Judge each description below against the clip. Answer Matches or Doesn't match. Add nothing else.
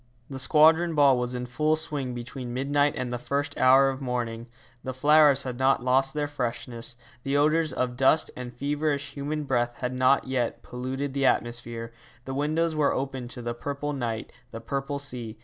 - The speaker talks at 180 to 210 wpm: Matches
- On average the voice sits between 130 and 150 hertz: Matches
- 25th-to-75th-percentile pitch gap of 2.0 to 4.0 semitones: Matches